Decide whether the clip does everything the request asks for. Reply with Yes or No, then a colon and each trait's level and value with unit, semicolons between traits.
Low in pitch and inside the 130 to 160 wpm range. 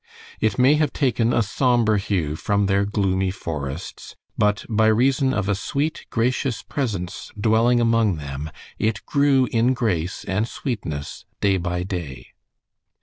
Yes: low, 105 Hz; average, 145 wpm